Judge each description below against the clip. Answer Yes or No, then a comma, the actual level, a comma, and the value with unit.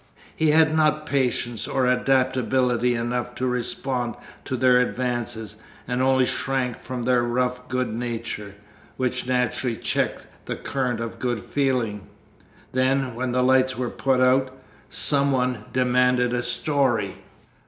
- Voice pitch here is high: No, low, 125 Hz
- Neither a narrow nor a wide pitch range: No, narrow, 1.4 semitones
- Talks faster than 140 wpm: No, slow, 135 wpm